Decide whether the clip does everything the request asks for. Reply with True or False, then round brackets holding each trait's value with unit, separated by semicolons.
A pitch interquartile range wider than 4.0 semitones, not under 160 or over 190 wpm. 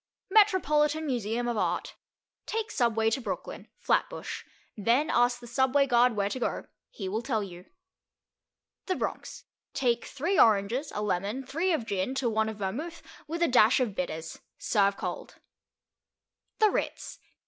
False (5.4 semitones; 150 wpm)